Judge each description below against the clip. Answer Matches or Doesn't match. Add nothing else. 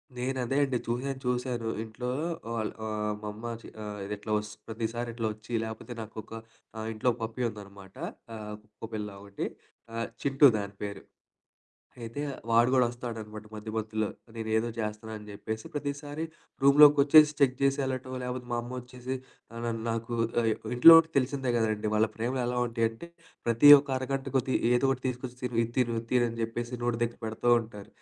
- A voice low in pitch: Matches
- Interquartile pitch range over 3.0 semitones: Doesn't match